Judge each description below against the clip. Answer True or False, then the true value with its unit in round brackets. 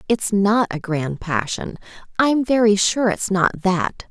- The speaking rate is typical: True (160 wpm)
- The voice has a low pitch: False (200 Hz)